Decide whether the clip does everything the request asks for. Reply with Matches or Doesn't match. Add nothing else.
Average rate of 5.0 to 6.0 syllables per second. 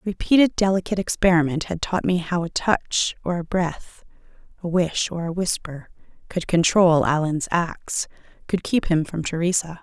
Doesn't match